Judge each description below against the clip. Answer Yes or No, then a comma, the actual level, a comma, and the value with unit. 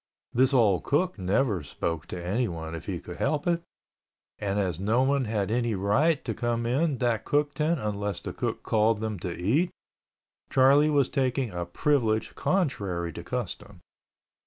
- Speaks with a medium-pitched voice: No, low, 115 Hz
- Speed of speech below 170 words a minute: Yes, average, 160 wpm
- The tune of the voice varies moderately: No, wide, 6.1 semitones